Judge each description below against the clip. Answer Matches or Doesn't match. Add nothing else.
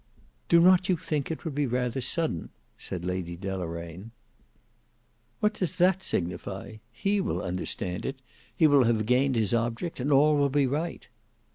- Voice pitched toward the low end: Matches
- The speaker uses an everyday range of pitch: Doesn't match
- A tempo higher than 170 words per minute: Doesn't match